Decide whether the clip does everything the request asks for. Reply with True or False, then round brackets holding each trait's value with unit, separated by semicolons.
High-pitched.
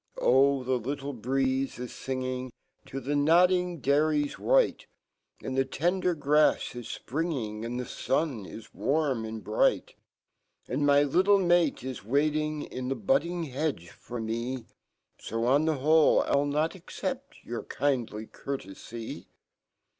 False (140 Hz)